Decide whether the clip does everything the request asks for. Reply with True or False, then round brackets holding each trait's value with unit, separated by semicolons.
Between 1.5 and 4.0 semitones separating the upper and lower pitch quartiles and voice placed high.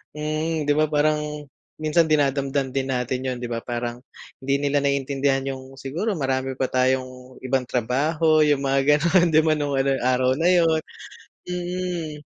False (2.8 semitones; 140 Hz)